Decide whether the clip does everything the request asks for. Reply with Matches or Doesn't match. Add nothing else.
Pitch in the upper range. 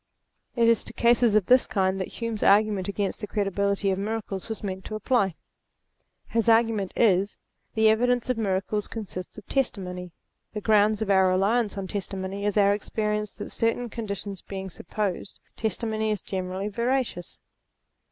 Matches